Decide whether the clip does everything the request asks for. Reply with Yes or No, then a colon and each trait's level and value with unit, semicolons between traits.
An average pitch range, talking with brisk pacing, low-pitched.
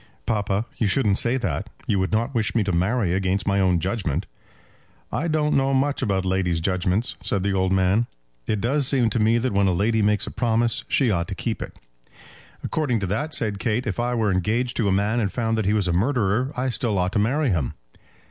Yes: average, 4.0 semitones; fast, 225 wpm; low, 105 Hz